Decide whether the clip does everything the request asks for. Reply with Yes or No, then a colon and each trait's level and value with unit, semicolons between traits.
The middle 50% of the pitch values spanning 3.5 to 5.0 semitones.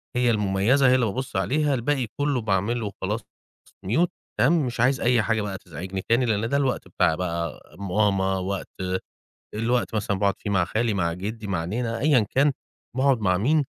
Yes: average, 4.7 semitones